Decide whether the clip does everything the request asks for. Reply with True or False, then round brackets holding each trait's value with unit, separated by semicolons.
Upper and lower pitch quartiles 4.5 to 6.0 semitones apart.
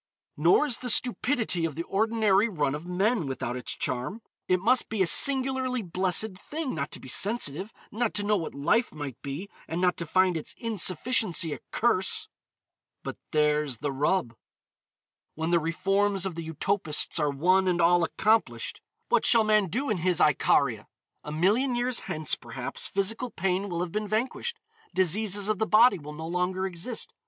True (5.3 semitones)